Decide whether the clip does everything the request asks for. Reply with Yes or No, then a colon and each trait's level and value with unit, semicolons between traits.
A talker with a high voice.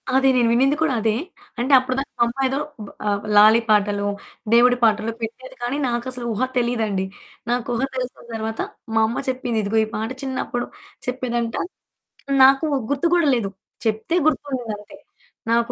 Yes: high, 240 Hz